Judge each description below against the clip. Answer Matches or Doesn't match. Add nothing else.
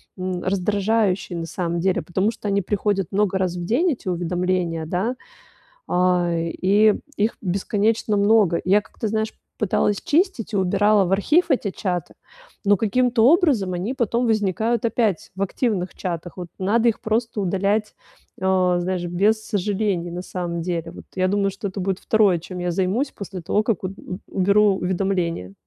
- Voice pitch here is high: Matches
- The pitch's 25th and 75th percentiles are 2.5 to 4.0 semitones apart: Matches